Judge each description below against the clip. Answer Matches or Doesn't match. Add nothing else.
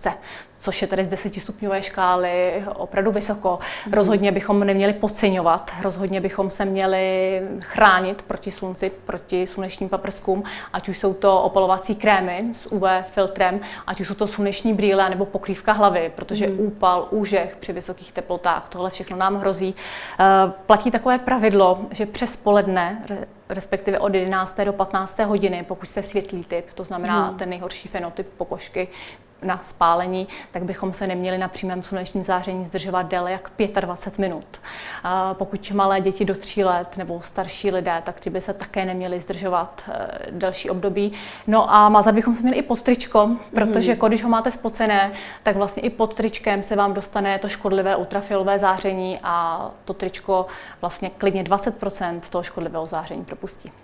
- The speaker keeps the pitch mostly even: Matches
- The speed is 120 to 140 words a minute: Doesn't match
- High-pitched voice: Matches